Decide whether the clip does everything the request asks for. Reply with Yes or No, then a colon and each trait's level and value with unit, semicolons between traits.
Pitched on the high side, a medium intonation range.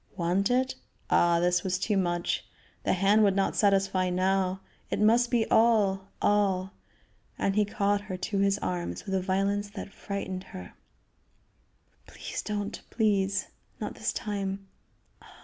No: high, 195 Hz; narrow, 1.7 semitones